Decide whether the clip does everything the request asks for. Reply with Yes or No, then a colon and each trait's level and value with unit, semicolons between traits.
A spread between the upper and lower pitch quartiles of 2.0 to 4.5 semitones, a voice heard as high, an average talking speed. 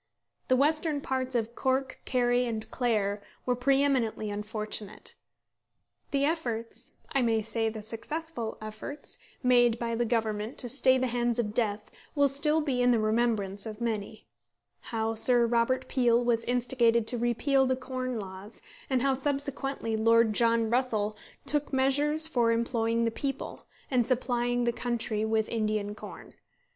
Yes: average, 2.7 semitones; high, 240 Hz; average, 150 wpm